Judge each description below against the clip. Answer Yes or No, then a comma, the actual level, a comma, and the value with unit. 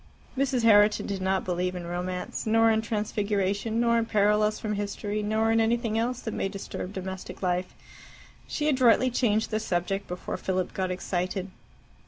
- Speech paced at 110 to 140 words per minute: No, average, 165 wpm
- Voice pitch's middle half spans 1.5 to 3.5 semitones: Yes, average, 3.2 semitones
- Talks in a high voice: Yes, high, 210 Hz